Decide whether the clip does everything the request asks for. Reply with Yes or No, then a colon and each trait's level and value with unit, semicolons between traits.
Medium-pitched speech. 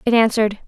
No: high, 220 Hz